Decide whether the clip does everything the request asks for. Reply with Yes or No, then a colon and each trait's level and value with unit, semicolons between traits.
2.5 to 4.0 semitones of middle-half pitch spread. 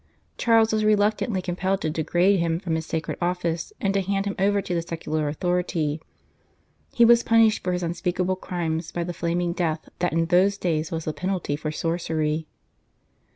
Yes: average, 3.1 semitones